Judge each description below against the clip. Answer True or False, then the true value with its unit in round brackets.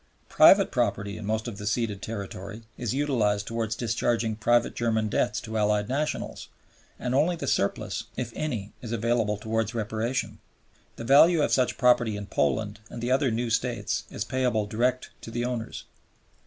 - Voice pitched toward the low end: True (115 Hz)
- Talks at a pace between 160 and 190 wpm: True (170 wpm)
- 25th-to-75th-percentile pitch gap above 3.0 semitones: False (2.7 semitones)